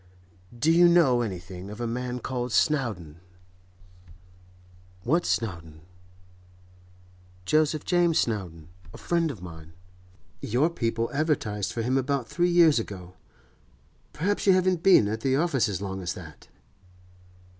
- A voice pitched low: Yes, low, 120 Hz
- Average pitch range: No, wide, 8.5 semitones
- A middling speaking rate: No, slow, 125 wpm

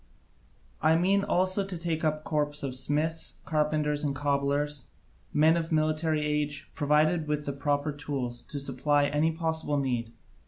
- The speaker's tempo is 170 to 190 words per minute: No, average, 150 wpm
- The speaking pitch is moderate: Yes, medium, 150 Hz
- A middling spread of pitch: No, narrow, 1.8 semitones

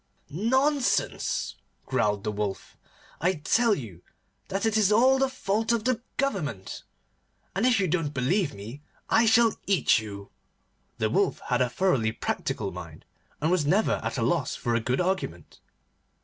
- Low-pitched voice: No, medium, 185 Hz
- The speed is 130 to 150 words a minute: No, average, 160 wpm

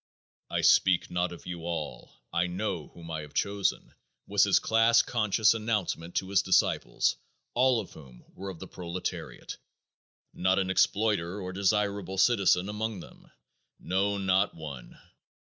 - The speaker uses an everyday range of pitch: Yes, average, 3.1 semitones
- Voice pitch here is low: Yes, very low, 95 Hz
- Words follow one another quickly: No, average, 145 wpm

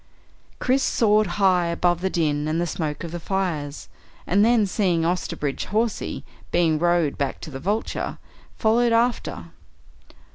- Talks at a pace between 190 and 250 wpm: No, average, 145 wpm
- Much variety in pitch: No, average, 4.6 semitones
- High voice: No, medium, 175 Hz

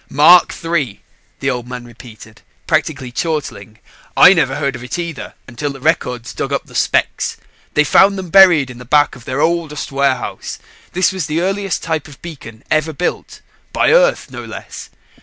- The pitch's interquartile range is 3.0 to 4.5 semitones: No, average, 5.3 semitones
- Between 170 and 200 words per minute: Yes, average, 175 wpm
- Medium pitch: Yes, medium, 145 Hz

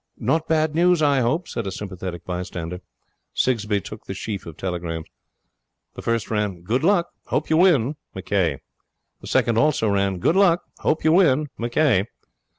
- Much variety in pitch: Yes, wide, 8.7 semitones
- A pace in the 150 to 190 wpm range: Yes, average, 160 wpm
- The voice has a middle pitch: No, low, 115 Hz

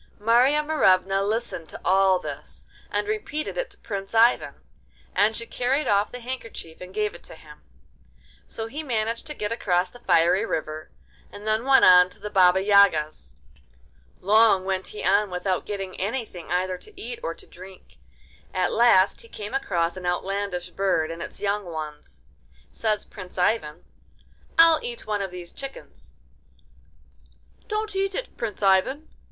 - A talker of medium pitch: No, high, 205 Hz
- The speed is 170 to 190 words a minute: No, average, 160 wpm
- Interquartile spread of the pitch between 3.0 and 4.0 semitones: No, average, 4.7 semitones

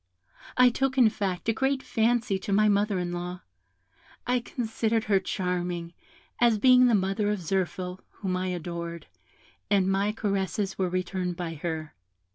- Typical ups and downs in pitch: Yes, average, 3.6 semitones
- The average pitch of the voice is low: No, high, 195 Hz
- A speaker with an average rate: Yes, average, 155 wpm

